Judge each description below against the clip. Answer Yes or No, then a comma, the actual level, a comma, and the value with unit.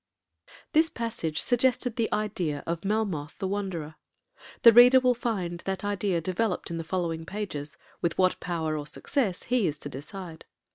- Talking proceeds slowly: No, average, 160 wpm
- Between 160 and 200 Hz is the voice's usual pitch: Yes, high, 190 Hz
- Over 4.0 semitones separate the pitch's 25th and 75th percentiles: Yes, wide, 5.4 semitones